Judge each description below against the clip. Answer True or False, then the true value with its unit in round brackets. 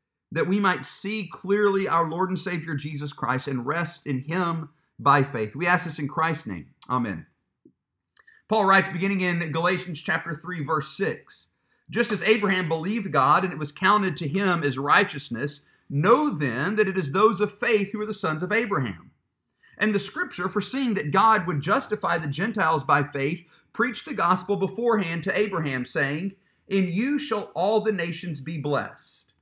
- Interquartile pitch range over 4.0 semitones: True (5.0 semitones)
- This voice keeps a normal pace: True (175 wpm)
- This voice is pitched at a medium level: True (180 Hz)